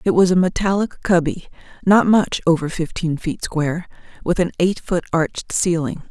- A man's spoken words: No, female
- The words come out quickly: No, average, 165 wpm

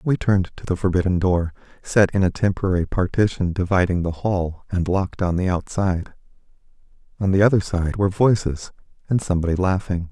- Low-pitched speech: Yes, very low, 95 Hz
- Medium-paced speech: Yes, average, 165 wpm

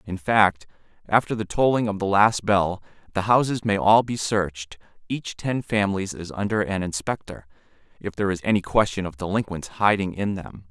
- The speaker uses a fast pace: No, average, 170 wpm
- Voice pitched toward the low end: Yes, low, 100 Hz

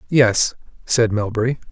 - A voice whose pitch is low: Yes, low, 115 Hz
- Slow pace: Yes, slow, 105 wpm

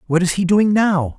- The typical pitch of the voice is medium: Yes, medium, 180 Hz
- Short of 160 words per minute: No, fast, 255 wpm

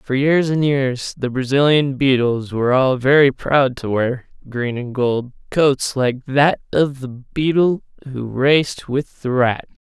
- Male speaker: Yes, male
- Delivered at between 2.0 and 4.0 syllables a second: Yes, 3.8 syllables/s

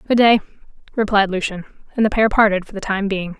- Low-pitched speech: No, high, 205 Hz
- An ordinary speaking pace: No, fast, 210 wpm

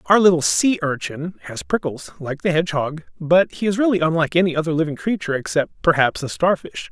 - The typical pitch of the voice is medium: Yes, medium, 160 Hz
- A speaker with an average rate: Yes, average, 190 wpm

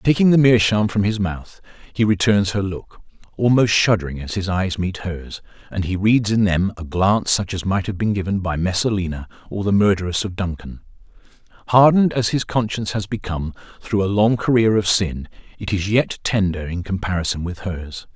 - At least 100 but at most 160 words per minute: No, average, 185 wpm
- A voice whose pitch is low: Yes, low, 100 Hz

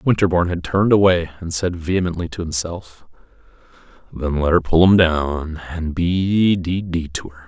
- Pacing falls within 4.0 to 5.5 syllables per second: Yes, 4.9 syllables/s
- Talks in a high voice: No, very low, 85 Hz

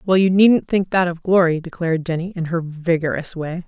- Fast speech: Yes, fast, 210 wpm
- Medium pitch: Yes, medium, 175 Hz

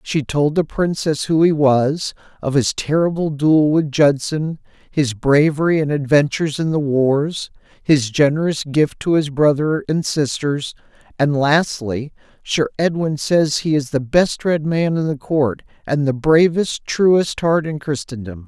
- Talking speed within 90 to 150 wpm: No, average, 160 wpm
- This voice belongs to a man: Yes, male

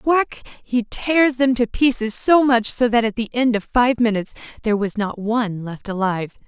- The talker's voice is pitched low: No, high, 230 Hz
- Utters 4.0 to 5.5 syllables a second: Yes, 5.0 syllables/s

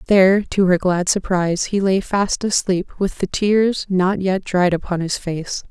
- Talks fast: No, average, 190 wpm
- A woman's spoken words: Yes, female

